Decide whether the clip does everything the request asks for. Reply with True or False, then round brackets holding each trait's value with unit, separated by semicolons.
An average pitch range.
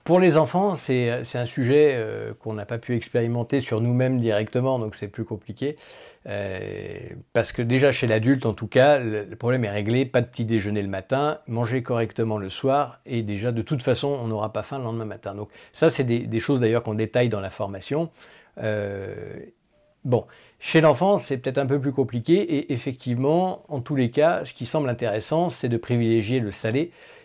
True (4.1 semitones)